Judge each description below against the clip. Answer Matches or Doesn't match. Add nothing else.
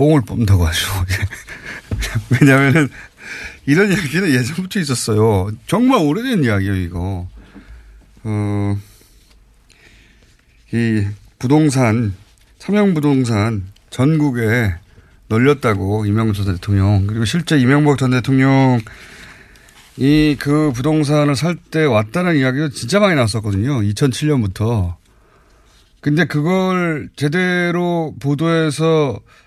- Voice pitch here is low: Matches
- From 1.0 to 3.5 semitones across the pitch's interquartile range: Doesn't match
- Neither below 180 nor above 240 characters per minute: Matches